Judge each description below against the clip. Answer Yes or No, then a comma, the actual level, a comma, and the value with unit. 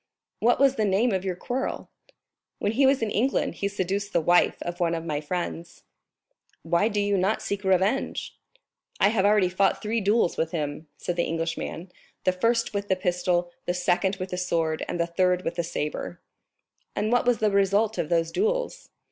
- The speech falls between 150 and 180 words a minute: No, average, 195 wpm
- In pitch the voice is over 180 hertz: Yes, high, 190 Hz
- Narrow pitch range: No, average, 3.4 semitones